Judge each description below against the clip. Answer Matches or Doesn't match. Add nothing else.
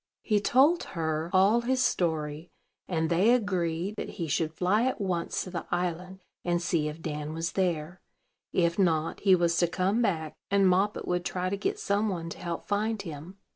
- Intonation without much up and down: Doesn't match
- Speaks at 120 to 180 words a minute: Doesn't match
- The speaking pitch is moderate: Matches